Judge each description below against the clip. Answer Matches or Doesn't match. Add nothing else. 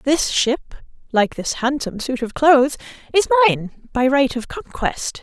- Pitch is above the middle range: Matches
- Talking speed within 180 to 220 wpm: Doesn't match